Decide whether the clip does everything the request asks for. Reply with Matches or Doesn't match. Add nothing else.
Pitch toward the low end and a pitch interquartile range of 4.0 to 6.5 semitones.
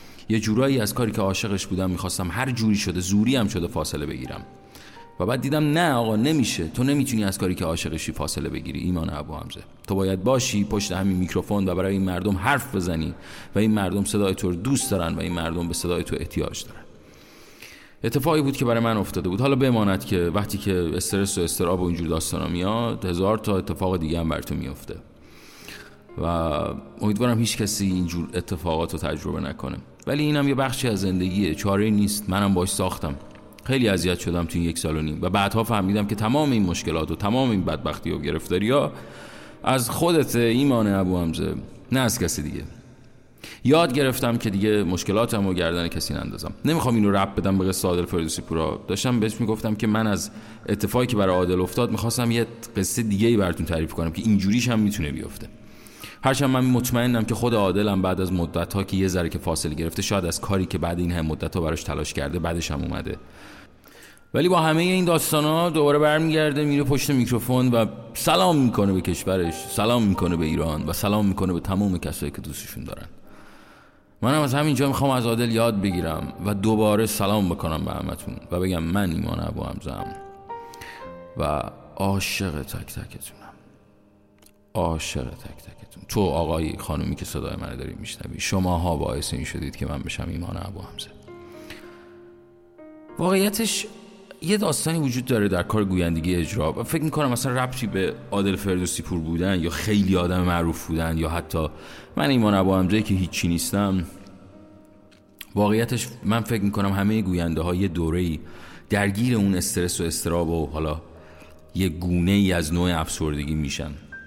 Matches